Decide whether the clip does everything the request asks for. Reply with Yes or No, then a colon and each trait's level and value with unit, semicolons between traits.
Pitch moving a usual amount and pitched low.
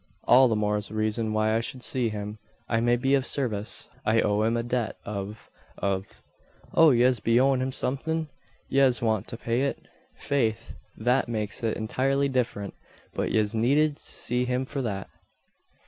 Yes: average, 3.3 semitones; low, 120 Hz